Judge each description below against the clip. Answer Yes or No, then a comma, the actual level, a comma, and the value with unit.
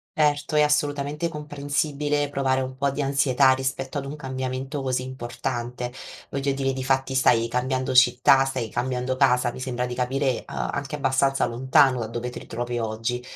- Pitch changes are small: Yes, narrow, 2.0 semitones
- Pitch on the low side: Yes, low, 130 Hz